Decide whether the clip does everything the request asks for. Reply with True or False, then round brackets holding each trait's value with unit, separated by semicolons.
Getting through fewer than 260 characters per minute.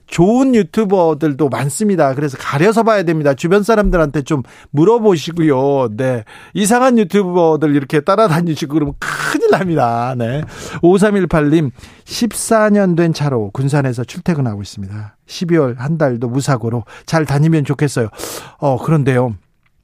False (305 characters per minute)